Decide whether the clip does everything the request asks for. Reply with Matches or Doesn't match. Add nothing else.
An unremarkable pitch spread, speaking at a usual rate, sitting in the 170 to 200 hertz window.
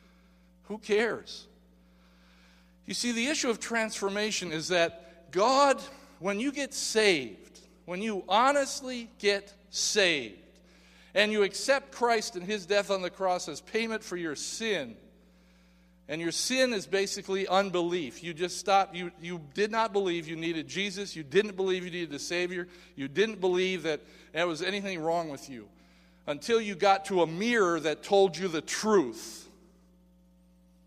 Matches